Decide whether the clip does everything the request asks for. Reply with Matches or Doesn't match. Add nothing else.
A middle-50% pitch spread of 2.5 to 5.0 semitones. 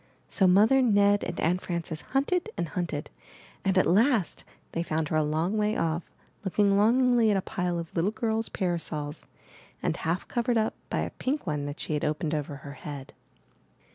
Doesn't match